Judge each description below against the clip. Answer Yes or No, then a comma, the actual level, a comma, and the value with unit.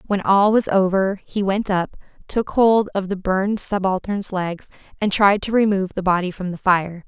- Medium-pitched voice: No, high, 195 Hz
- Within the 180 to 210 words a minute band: Yes, average, 195 wpm